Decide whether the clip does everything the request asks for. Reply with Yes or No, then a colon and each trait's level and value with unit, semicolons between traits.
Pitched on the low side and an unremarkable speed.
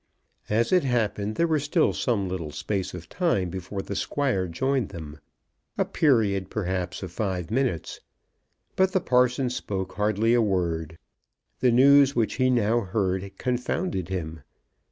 Yes: low, 105 Hz; average, 150 wpm